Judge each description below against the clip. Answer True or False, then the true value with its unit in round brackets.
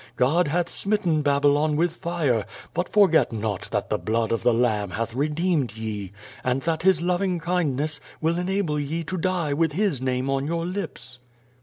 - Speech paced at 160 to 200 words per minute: True (170 wpm)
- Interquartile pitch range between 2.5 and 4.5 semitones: False (5.6 semitones)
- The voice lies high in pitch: False (150 Hz)